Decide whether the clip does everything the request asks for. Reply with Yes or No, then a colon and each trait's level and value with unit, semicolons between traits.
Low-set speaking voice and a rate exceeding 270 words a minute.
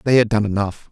No: low, 105 Hz; fast, 265 wpm